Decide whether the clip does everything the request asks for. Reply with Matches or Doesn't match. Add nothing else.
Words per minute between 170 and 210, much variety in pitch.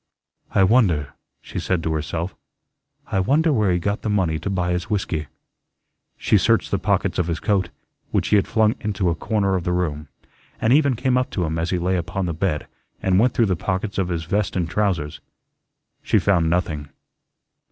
Doesn't match